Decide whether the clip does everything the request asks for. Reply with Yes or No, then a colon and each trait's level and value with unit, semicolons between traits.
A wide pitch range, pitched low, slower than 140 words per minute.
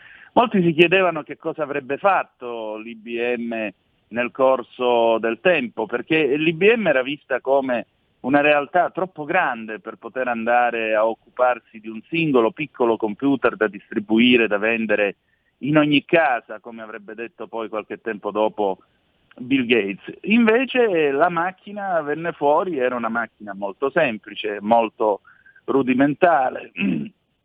Yes: wide, 6.4 semitones; low, 125 Hz; average, 130 wpm